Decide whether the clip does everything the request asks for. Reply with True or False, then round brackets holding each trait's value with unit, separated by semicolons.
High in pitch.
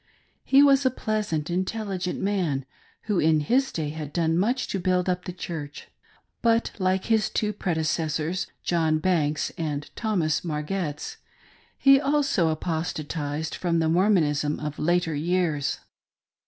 False (175 Hz)